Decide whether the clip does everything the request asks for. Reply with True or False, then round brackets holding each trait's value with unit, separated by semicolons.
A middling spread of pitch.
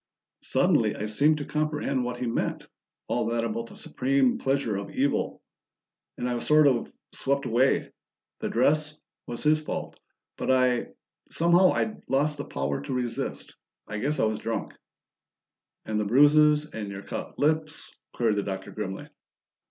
True (5.0 semitones)